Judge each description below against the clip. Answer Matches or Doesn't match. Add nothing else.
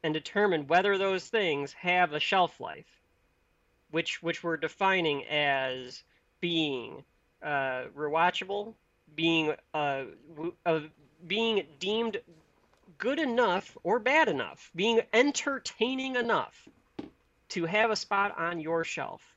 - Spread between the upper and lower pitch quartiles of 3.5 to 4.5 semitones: Doesn't match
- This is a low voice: Doesn't match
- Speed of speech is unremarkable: Doesn't match